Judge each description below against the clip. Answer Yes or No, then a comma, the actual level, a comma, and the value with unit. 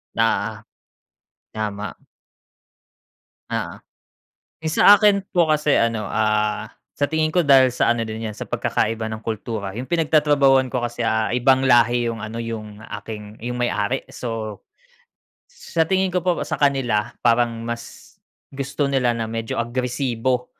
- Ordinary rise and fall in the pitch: Yes, average, 3.7 semitones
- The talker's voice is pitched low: Yes, low, 120 Hz